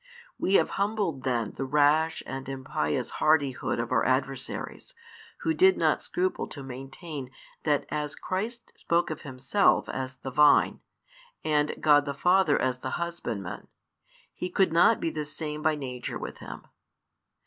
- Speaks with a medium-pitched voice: Yes, medium, 150 Hz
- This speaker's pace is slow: No, average, 150 wpm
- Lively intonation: No, average, 4.4 semitones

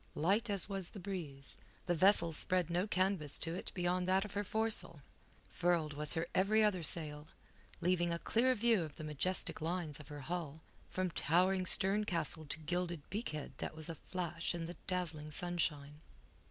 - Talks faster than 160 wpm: Yes, average, 175 wpm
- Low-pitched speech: No, medium, 175 Hz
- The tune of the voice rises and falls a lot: No, average, 3.3 semitones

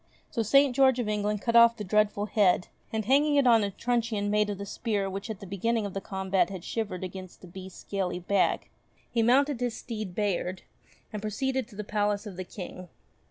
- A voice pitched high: Yes, high, 210 Hz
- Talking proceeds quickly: Yes, fast, 215 wpm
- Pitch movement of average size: Yes, average, 3.3 semitones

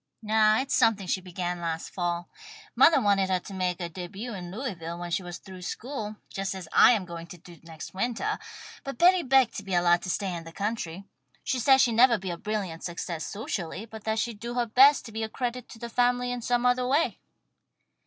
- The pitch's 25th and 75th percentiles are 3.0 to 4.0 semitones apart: No, wide, 5.4 semitones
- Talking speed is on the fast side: Yes, fast, 225 wpm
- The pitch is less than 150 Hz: No, high, 205 Hz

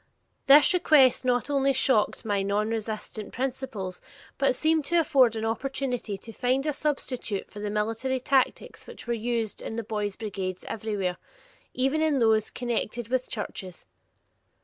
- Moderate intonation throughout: Yes, average, 4.1 semitones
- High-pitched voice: Yes, high, 235 Hz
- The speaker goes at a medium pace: Yes, average, 150 wpm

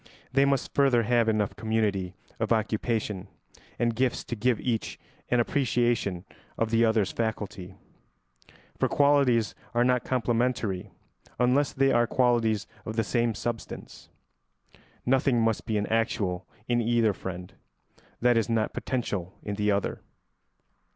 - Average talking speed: No, slow, 130 wpm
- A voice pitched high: No, low, 115 Hz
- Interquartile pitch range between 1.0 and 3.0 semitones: Yes, average, 2.7 semitones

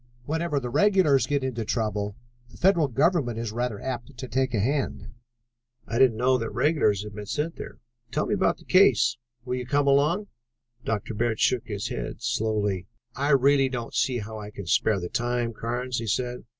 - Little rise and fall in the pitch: No, average, 4.1 semitones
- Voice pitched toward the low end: Yes, low, 125 Hz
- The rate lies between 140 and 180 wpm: No, average, 190 wpm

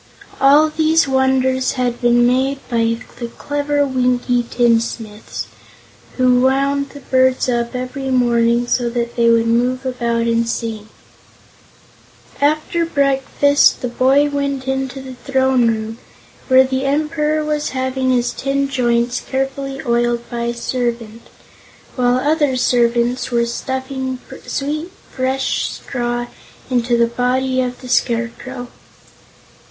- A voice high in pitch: Yes, very high, 255 Hz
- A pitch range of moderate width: No, narrow, 2.2 semitones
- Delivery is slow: Yes, slow, 125 wpm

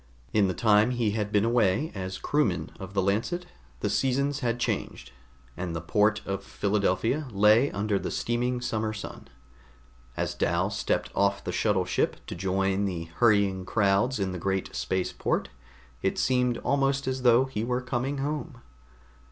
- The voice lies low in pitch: Yes, low, 105 Hz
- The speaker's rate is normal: Yes, average, 170 wpm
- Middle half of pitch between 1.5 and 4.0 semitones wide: No, average, 4.4 semitones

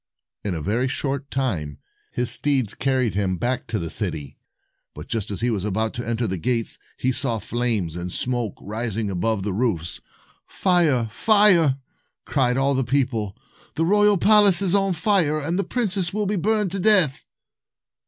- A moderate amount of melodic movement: No, wide, 8.3 semitones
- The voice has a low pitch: Yes, low, 125 Hz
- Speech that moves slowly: No, average, 175 wpm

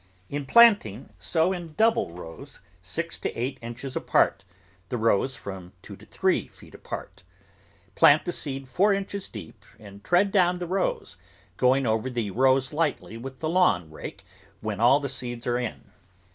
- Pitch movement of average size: No, wide, 7.5 semitones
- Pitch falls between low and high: No, low, 130 Hz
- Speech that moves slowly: No, average, 165 wpm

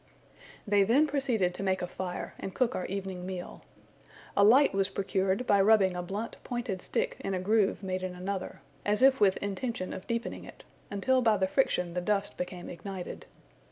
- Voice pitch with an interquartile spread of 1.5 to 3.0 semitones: No, average, 3.4 semitones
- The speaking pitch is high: Yes, high, 195 Hz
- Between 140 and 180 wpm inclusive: No, average, 190 wpm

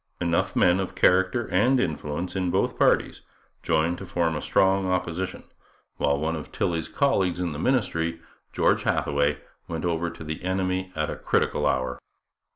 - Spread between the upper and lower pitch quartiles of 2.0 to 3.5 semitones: Yes, average, 2.9 semitones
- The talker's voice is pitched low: Yes, very low, 85 Hz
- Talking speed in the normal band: Yes, average, 160 wpm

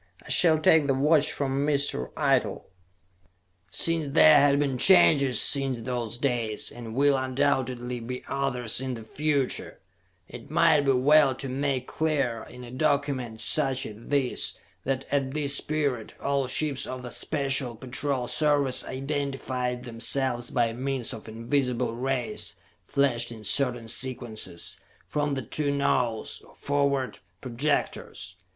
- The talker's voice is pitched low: Yes, low, 130 Hz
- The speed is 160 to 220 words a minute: No, average, 140 wpm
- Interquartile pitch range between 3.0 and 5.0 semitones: No, narrow, 2.6 semitones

